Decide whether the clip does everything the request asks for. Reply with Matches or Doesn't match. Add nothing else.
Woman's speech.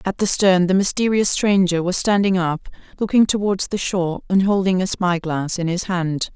Matches